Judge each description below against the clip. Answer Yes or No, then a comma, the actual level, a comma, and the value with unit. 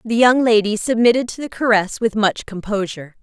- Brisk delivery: No, average, 185 wpm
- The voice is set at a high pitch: Yes, high, 220 Hz